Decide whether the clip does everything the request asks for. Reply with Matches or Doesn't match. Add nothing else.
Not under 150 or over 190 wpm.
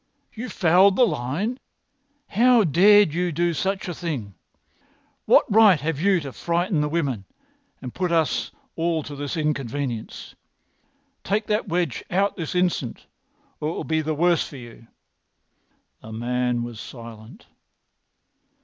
Doesn't match